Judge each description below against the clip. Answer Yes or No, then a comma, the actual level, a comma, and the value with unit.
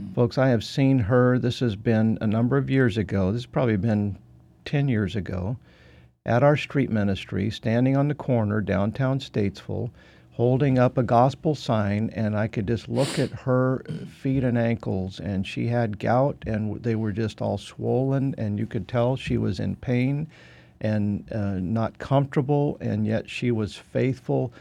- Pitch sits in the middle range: No, low, 115 Hz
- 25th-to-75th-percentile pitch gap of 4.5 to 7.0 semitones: No, average, 3.9 semitones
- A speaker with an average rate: Yes, average, 175 wpm